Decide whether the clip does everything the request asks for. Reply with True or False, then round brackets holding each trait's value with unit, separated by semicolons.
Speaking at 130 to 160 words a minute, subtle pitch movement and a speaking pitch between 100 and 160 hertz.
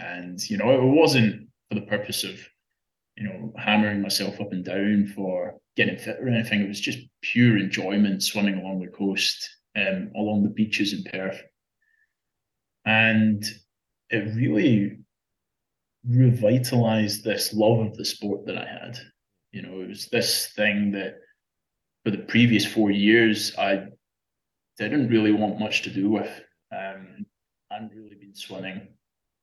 True (150 wpm; 2.2 semitones; 105 Hz)